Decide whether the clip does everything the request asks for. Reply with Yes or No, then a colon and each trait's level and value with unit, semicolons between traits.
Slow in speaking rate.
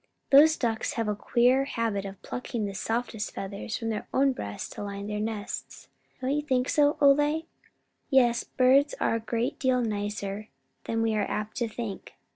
No: average, 180 wpm